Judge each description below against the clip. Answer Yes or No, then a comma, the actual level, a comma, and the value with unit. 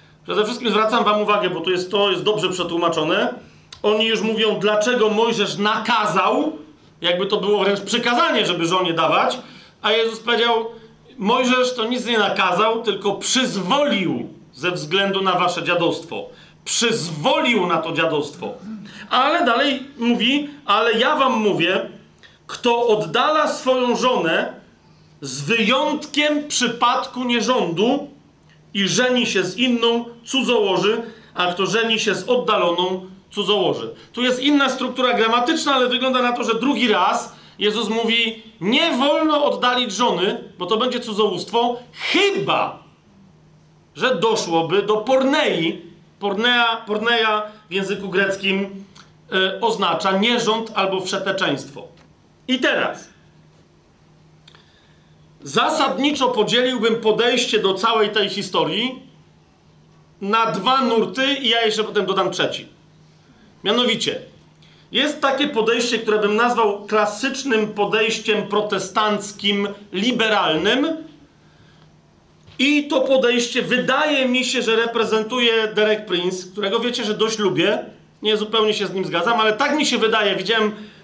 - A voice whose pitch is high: Yes, high, 220 Hz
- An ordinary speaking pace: Yes, average, 125 wpm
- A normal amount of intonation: Yes, average, 3.8 semitones